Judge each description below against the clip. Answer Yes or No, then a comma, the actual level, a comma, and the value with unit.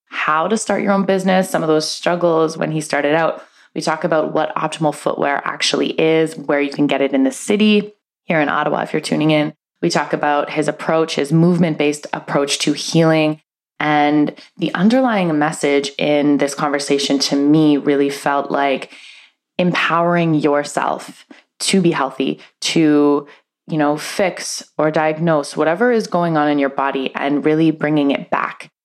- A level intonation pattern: Yes, narrow, 2.2 semitones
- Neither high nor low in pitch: Yes, medium, 155 Hz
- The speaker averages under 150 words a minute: No, average, 175 wpm